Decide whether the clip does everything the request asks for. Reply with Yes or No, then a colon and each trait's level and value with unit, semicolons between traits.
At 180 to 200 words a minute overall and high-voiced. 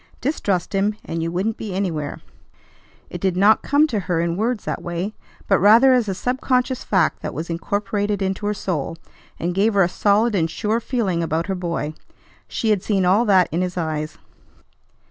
Yes: average, 190 wpm; high, 195 Hz